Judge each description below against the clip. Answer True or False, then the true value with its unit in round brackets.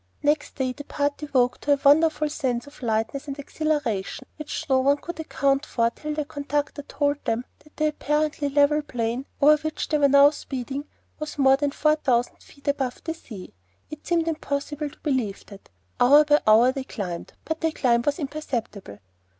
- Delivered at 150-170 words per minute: False (185 wpm)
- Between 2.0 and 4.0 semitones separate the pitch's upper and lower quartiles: True (2.8 semitones)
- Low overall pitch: False (285 Hz)